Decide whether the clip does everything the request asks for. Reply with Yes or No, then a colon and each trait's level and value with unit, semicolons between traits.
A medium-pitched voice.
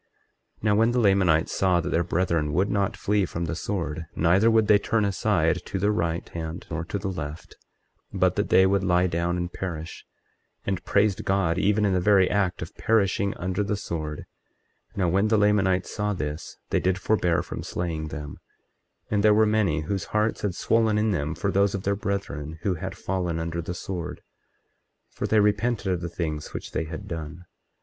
No: very low, 95 Hz